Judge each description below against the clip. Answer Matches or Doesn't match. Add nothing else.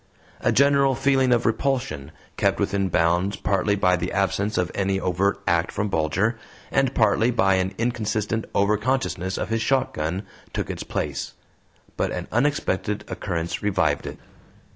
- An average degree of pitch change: Matches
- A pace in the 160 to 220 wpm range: Doesn't match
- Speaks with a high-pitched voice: Doesn't match